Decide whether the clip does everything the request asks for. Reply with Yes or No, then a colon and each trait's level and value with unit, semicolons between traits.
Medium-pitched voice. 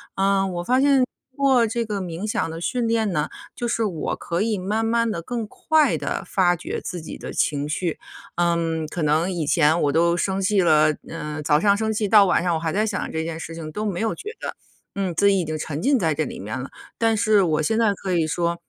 Yes: medium, 180 Hz